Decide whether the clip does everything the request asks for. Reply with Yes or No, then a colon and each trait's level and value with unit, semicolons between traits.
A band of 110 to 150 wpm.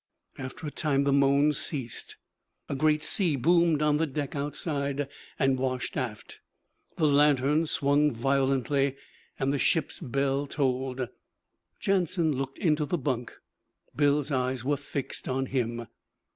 Yes: slow, 135 wpm